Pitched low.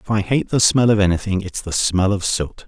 Yes: low, 100 Hz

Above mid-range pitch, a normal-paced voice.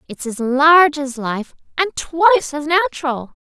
Yes: very high, 295 Hz; average, 155 wpm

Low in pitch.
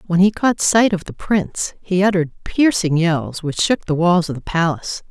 No: medium, 180 Hz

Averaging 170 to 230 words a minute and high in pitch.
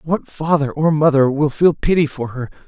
No: average, 200 wpm; medium, 145 Hz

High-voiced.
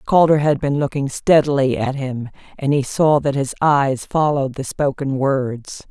No: medium, 140 Hz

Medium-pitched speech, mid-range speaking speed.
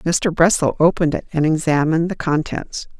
Yes: medium, 165 Hz; average, 160 wpm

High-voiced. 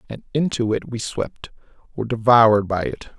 No: low, 115 Hz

